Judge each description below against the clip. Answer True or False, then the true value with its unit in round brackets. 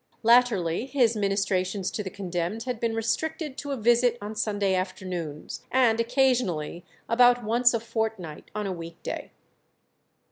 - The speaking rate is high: False (145 wpm)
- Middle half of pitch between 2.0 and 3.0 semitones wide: False (4.4 semitones)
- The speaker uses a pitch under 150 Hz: False (220 Hz)